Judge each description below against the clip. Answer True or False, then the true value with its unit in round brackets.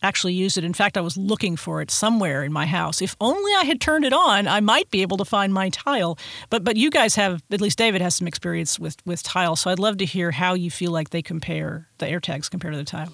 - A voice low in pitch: False (185 Hz)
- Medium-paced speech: False (275 wpm)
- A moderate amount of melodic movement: True (3.4 semitones)